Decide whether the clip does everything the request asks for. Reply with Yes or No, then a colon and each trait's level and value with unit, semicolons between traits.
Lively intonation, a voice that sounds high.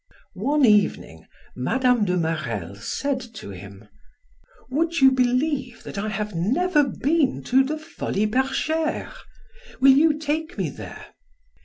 Yes: wide, 7.2 semitones; very high, 255 Hz